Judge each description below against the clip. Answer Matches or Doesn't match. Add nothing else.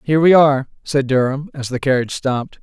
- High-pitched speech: Doesn't match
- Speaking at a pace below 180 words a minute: Doesn't match